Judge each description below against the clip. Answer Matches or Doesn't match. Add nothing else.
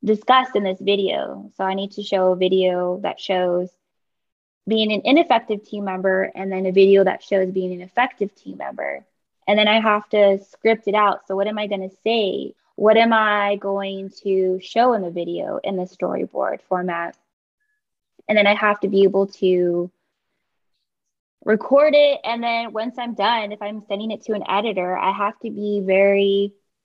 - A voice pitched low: Doesn't match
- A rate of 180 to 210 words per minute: Matches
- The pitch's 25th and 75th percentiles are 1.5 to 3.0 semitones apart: Matches